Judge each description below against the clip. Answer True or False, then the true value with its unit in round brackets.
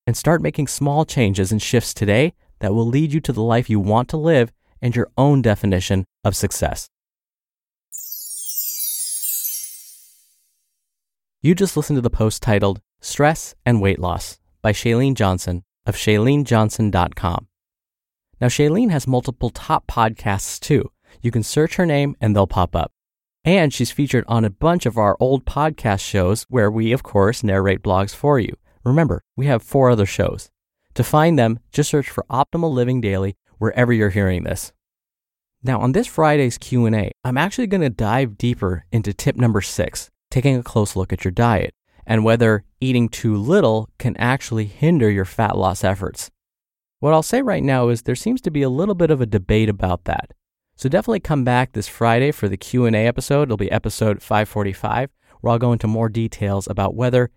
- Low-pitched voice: True (115 Hz)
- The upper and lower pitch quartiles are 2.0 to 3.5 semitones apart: False (4.9 semitones)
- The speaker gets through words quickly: False (175 wpm)